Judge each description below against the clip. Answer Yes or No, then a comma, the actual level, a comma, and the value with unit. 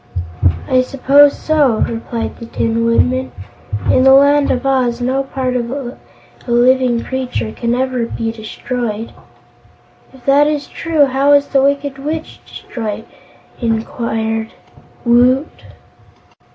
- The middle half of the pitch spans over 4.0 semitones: No, average, 2.9 semitones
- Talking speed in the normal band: No, slow, 125 wpm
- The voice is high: Yes, very high, 255 Hz